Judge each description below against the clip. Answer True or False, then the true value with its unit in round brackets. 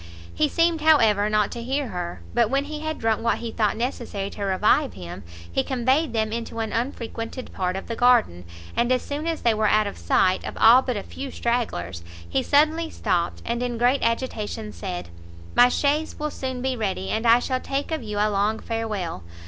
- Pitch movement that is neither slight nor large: True (4.0 semitones)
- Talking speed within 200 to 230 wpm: True (205 wpm)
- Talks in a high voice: True (230 Hz)